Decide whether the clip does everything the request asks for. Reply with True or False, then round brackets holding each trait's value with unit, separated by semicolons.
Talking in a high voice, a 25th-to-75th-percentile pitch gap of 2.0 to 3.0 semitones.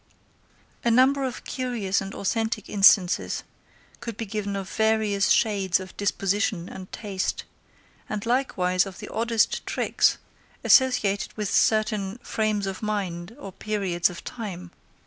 True (205 Hz; 2.6 semitones)